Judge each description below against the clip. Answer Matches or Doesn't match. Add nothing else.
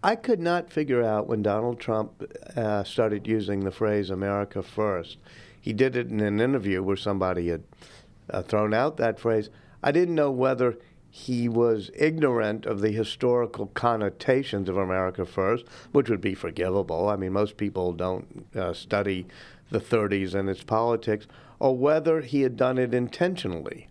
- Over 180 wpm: Doesn't match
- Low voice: Matches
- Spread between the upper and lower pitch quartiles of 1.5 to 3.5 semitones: Doesn't match